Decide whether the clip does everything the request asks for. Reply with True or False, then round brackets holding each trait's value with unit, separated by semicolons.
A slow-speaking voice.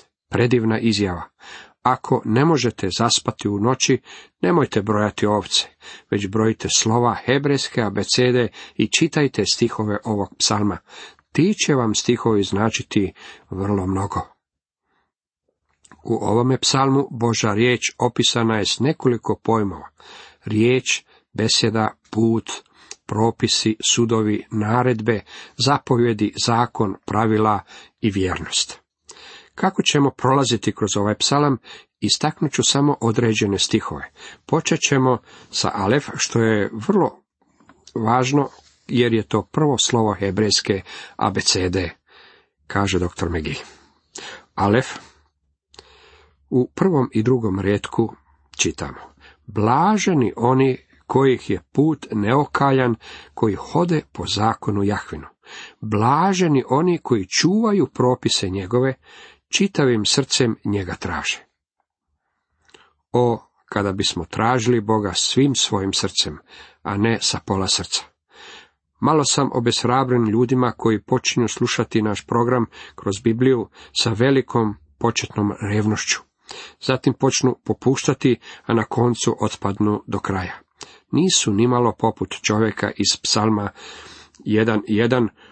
True (105 wpm)